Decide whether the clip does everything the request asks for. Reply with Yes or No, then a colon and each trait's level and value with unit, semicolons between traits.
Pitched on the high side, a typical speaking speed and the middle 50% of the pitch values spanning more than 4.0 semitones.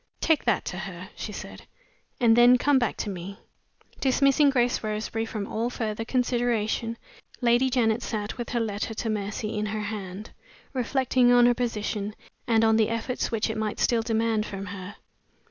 No: high, 225 Hz; average, 175 wpm; narrow, 2.4 semitones